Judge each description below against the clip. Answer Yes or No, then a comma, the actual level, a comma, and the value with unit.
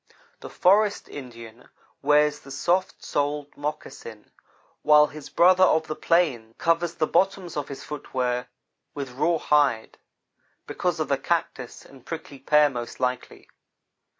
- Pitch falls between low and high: Yes, medium, 150 Hz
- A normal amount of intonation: Yes, average, 4.2 semitones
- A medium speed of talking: No, slow, 130 wpm